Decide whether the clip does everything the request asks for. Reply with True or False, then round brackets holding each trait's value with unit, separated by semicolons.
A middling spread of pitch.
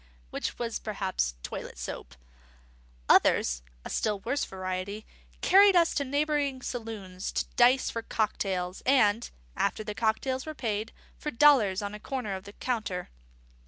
True (5.0 semitones)